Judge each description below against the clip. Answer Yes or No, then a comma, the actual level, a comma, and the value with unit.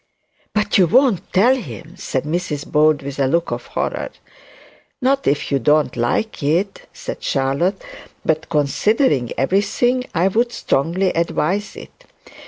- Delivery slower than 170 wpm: Yes, average, 140 wpm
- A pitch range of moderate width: No, wide, 6.3 semitones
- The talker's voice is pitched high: No, medium, 170 Hz